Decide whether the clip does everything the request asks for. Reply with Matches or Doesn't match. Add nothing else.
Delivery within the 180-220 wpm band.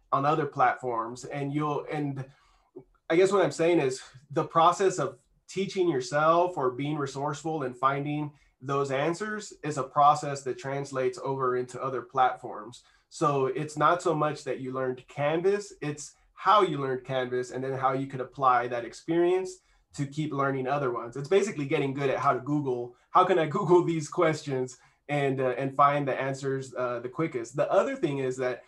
Matches